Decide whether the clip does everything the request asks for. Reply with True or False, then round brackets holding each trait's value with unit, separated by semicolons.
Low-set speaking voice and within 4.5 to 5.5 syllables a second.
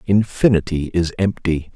True (90 Hz; 4.6 syllables/s)